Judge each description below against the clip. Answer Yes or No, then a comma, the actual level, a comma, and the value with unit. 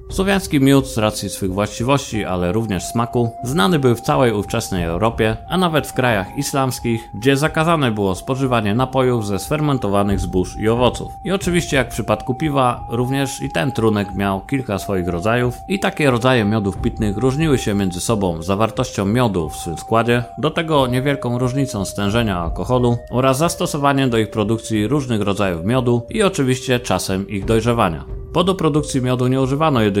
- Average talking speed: No, fast, 170 wpm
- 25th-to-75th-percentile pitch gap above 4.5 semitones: Yes, average, 5.0 semitones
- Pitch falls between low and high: No, low, 120 Hz